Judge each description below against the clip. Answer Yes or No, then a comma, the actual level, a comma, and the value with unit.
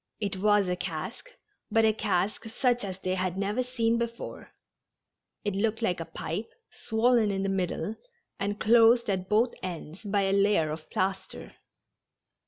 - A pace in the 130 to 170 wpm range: Yes, average, 160 wpm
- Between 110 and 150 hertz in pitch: No, high, 205 Hz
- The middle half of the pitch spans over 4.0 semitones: No, average, 3.2 semitones